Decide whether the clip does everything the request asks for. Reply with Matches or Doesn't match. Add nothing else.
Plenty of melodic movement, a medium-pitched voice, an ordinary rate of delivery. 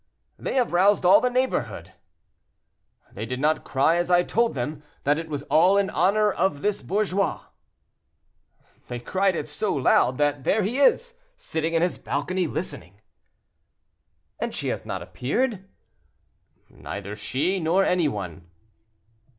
Matches